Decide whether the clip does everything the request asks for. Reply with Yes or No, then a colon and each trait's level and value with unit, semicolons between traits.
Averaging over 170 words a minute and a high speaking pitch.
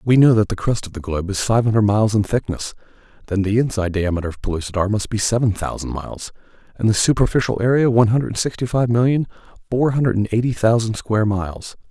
No: average, 200 wpm; low, 110 Hz